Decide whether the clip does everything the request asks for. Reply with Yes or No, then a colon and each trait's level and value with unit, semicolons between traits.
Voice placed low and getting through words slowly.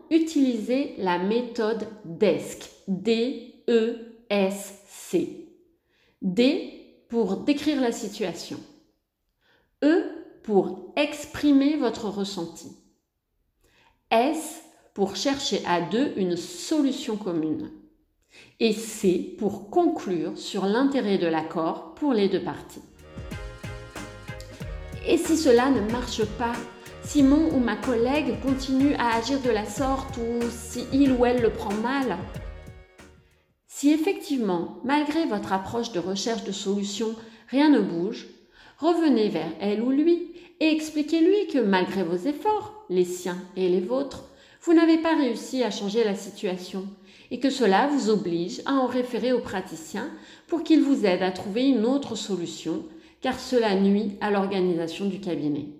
No: high, 230 Hz; slow, 130 wpm